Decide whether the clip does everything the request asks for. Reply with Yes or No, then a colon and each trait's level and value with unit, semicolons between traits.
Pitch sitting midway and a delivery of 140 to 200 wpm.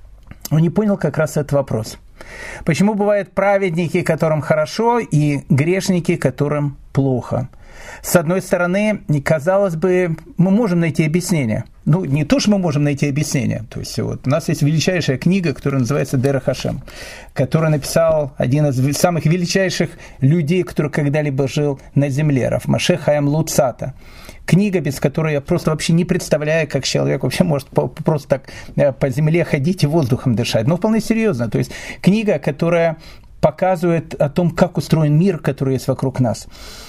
Yes: medium, 155 Hz; fast, 160 wpm